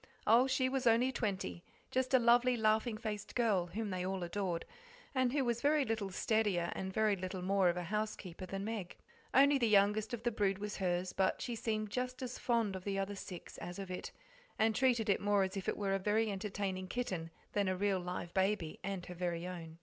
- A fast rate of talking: Yes, fast, 220 wpm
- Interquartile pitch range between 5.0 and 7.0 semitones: No, average, 3.6 semitones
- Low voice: No, high, 205 Hz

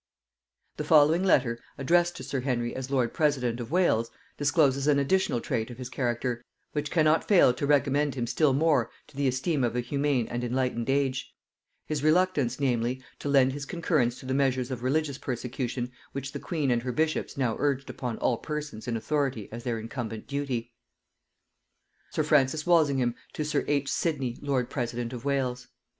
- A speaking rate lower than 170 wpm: No, average, 180 wpm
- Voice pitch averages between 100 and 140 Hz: Yes, low, 135 Hz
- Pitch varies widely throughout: No, average, 3.2 semitones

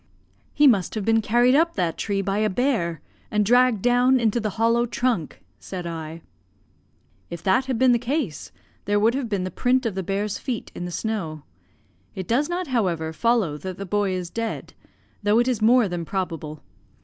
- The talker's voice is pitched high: Yes, high, 210 Hz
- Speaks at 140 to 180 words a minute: No, average, 195 wpm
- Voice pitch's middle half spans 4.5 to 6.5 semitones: Yes, average, 5.0 semitones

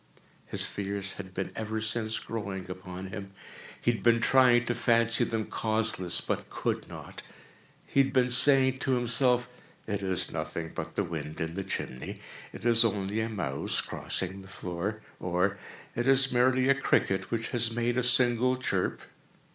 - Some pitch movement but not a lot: Yes, average, 4.2 semitones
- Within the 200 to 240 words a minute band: No, average, 165 wpm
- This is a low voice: Yes, low, 110 Hz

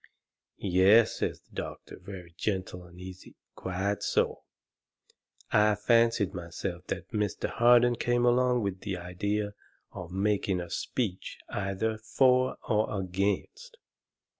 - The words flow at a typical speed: No, slow, 120 wpm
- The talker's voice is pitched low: Yes, low, 100 Hz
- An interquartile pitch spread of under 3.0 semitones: No, average, 3.7 semitones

